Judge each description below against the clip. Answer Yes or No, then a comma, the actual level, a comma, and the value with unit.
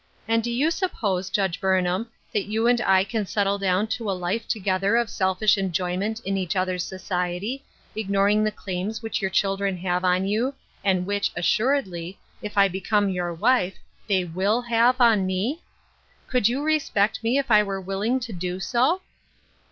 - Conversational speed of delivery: Yes, average, 175 wpm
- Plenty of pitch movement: No, average, 3.5 semitones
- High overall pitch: Yes, high, 200 Hz